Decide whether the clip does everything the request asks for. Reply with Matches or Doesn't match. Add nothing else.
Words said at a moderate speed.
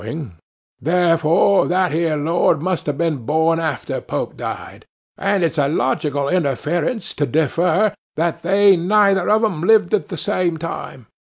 Matches